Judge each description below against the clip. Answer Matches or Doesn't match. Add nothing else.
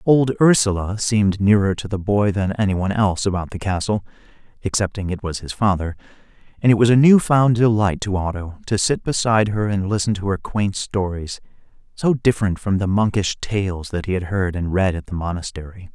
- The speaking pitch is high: Doesn't match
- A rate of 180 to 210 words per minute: Matches